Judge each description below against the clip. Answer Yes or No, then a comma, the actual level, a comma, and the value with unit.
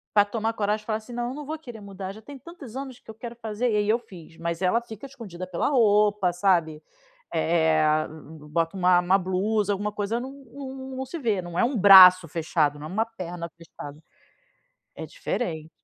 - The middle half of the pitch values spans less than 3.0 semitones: No, average, 5.1 semitones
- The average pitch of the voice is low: No, high, 205 Hz